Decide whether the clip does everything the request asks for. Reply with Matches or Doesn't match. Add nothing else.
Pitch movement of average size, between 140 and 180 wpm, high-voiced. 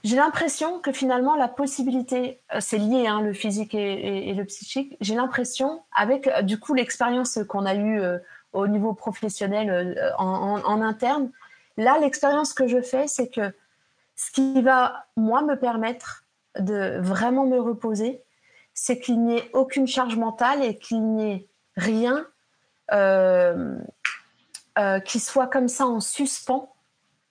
Matches